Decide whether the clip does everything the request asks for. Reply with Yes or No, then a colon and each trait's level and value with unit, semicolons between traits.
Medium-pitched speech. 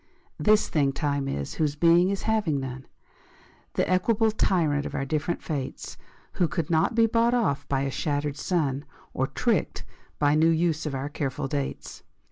Yes: medium, 150 Hz